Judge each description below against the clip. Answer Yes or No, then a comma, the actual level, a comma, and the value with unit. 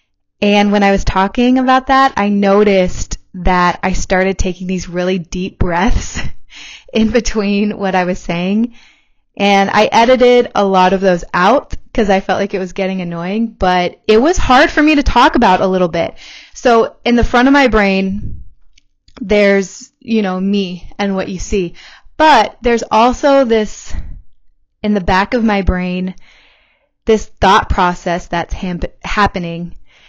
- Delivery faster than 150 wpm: Yes, average, 165 wpm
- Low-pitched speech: No, high, 200 Hz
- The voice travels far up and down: No, average, 3.8 semitones